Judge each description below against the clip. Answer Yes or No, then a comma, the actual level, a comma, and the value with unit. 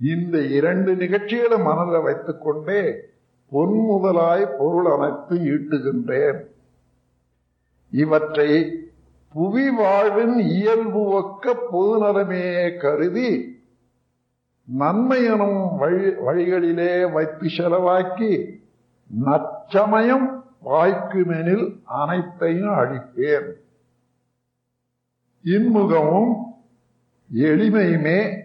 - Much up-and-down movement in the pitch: Yes, wide, 5.7 semitones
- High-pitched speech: No, medium, 175 Hz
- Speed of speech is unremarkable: No, slow, 60 wpm